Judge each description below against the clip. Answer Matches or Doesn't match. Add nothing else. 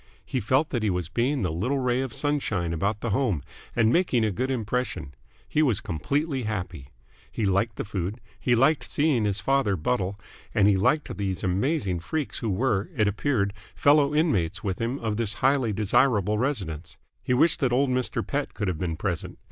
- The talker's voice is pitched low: Matches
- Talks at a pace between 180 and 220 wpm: Matches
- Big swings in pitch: Matches